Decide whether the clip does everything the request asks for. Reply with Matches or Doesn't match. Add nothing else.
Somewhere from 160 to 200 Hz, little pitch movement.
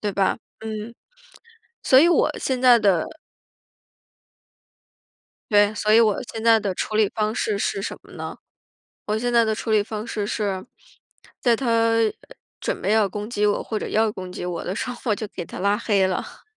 Doesn't match